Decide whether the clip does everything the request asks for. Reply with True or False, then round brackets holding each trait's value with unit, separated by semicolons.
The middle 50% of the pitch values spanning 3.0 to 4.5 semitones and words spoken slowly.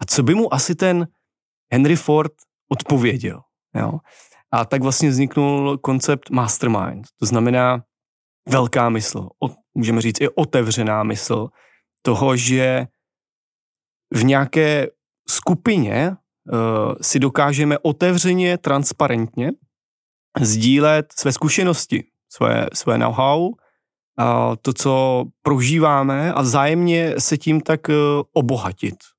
True (3.9 semitones; 105 wpm)